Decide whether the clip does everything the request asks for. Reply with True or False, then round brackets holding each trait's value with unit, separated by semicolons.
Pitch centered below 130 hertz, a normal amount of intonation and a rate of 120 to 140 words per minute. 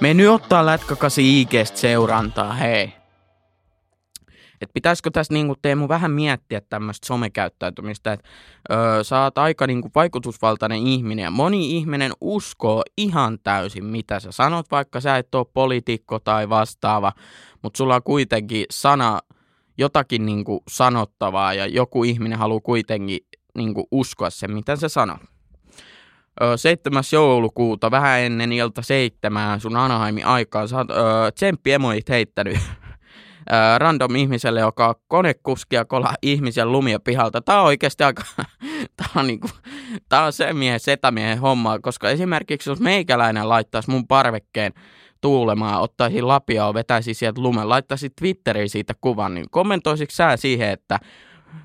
True (120 Hz; 4.3 semitones; 135 wpm)